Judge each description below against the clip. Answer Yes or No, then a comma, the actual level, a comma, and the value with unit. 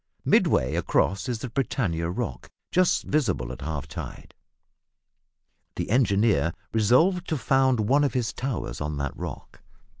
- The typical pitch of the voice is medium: No, low, 110 Hz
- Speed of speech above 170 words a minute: No, average, 140 wpm